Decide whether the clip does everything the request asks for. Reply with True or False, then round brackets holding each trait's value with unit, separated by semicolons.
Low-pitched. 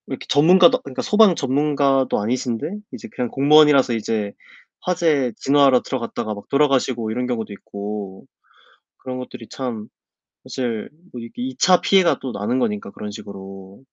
True (125 Hz)